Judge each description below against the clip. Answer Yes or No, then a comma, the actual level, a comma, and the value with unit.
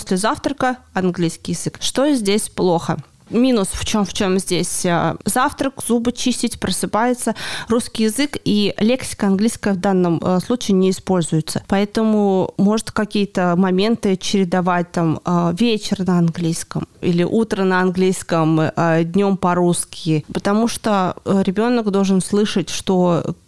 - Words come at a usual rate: Yes, average, 125 wpm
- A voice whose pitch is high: Yes, high, 195 Hz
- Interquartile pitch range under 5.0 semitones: Yes, average, 3.6 semitones